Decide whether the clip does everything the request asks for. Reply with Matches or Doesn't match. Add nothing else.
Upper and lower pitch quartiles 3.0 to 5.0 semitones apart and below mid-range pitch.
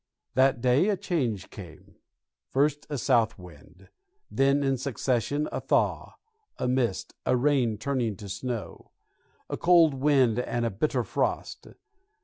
Matches